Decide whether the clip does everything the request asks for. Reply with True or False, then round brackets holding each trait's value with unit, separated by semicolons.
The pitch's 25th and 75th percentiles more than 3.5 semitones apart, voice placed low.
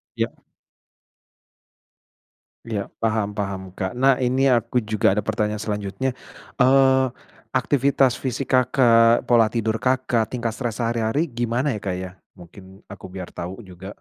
True (4.0 semitones; 115 Hz)